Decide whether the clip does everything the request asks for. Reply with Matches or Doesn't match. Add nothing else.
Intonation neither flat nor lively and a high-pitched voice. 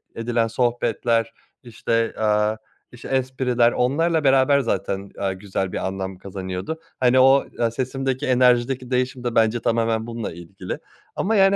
Doesn't match